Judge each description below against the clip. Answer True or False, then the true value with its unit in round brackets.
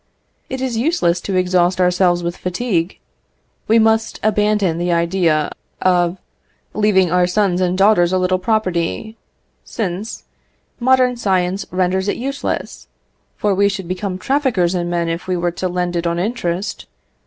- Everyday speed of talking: True (150 wpm)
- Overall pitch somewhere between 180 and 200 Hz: True (185 Hz)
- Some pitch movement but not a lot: True (3.3 semitones)